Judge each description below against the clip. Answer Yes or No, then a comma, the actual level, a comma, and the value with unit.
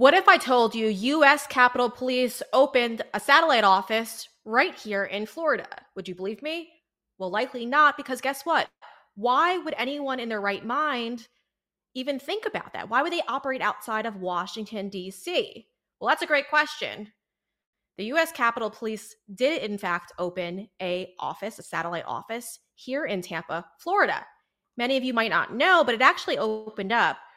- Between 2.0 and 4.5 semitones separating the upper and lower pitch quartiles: No, wide, 5.4 semitones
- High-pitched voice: Yes, high, 235 Hz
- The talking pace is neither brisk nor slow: Yes, average, 170 wpm